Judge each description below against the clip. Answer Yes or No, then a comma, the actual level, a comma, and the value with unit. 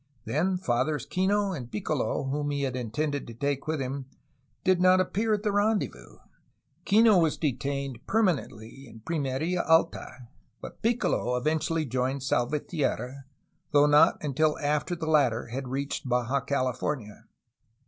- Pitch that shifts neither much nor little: Yes, average, 4.6 semitones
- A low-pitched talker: No, medium, 145 Hz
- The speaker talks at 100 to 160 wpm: Yes, average, 140 wpm